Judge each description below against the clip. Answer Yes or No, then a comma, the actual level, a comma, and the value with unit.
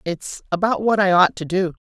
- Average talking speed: No, fast, 225 wpm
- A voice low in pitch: No, medium, 185 Hz